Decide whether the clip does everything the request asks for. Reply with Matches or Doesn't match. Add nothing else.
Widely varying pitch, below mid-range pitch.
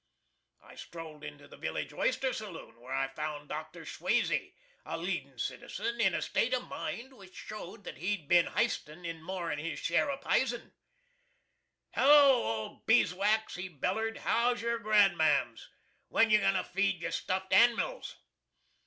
Doesn't match